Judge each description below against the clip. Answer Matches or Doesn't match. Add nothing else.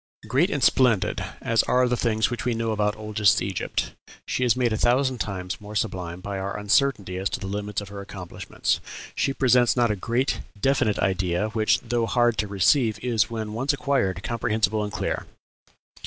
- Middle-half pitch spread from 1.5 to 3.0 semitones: Doesn't match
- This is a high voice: Doesn't match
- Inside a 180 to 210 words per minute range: Matches